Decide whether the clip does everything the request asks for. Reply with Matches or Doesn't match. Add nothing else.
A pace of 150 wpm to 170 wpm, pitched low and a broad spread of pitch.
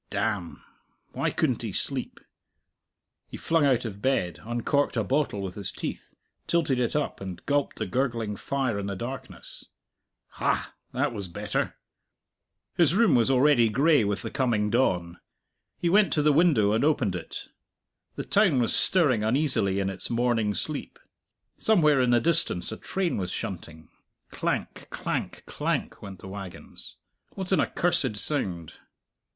Matches